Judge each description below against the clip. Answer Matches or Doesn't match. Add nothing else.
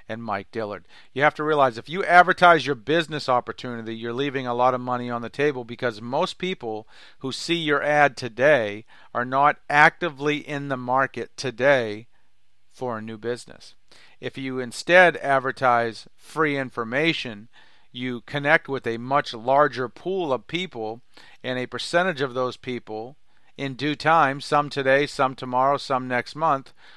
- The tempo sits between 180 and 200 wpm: Doesn't match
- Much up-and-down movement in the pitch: Doesn't match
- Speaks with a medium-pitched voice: Doesn't match